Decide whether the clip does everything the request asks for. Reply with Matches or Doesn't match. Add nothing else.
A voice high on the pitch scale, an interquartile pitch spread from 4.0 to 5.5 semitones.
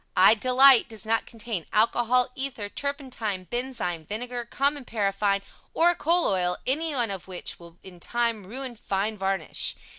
Matches